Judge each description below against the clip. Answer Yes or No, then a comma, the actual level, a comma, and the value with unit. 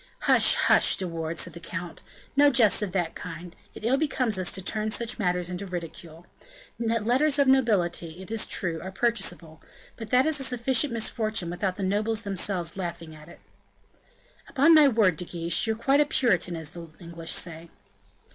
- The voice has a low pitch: No, high, 190 Hz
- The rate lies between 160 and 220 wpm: Yes, average, 185 wpm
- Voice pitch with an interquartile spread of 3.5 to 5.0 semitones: No, wide, 5.4 semitones